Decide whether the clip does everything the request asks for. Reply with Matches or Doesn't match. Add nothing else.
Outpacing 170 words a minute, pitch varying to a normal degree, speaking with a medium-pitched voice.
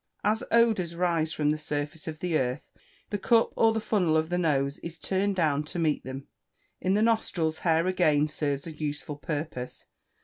Matches